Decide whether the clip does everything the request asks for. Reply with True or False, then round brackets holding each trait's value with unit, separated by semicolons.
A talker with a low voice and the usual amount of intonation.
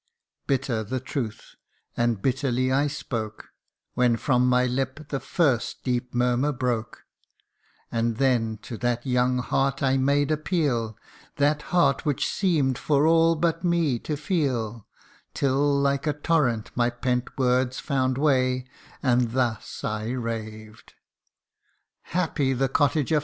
True (130 Hz; 3.1 semitones)